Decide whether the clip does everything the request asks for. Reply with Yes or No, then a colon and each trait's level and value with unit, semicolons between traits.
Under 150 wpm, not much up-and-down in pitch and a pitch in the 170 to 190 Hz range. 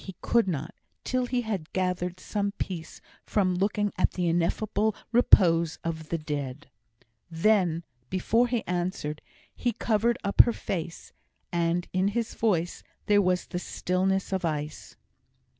No: average, 140 wpm; average, 3.8 semitones; medium, 185 Hz